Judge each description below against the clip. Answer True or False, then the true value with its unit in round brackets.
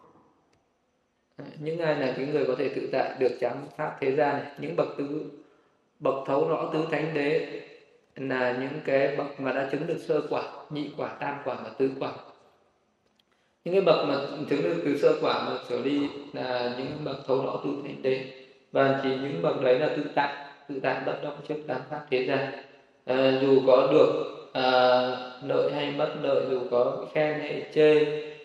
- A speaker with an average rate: True (195 wpm)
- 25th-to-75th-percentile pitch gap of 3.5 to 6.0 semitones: False (2.4 semitones)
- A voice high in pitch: False (140 Hz)